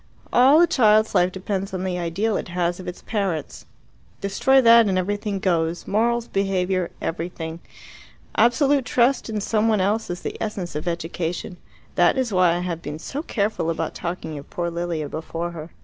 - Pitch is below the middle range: No, medium, 185 Hz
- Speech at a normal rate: Yes, average, 180 wpm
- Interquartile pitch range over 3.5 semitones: Yes, average, 4.2 semitones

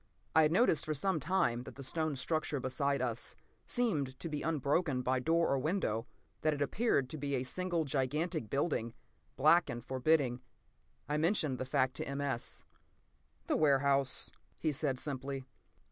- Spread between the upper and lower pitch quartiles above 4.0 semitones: No, average, 3.5 semitones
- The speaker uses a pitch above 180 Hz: No, medium, 140 Hz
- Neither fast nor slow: Yes, average, 160 wpm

